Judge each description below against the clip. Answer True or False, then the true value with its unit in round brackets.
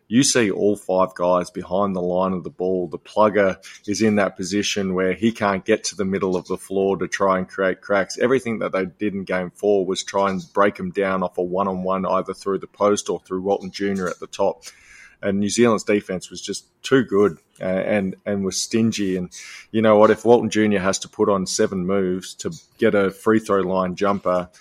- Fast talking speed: True (225 wpm)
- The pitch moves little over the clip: True (1.8 semitones)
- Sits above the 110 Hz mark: False (95 Hz)